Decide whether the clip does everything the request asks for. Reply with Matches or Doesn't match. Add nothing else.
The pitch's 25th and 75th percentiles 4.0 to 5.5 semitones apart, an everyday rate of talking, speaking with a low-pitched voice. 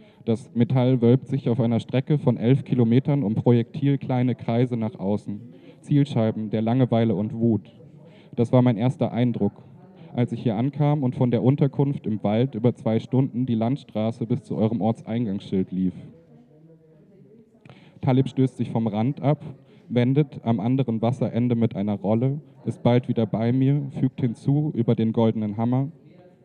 Doesn't match